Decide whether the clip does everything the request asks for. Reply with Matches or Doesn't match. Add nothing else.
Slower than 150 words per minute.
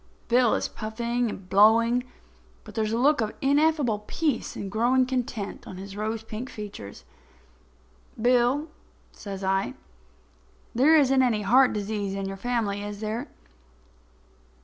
Matches